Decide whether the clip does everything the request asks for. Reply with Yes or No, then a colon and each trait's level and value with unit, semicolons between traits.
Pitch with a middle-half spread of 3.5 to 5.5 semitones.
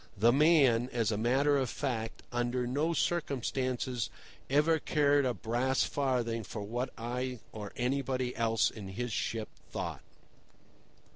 No: average, 3.0 semitones